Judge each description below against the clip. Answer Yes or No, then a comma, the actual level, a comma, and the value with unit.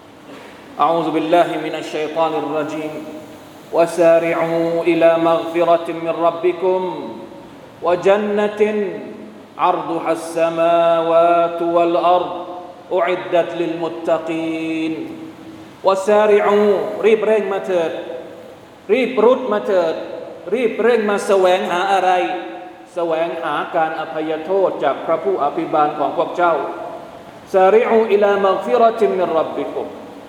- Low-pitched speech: No, medium, 170 Hz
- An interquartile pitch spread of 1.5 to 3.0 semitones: Yes, narrow, 2.5 semitones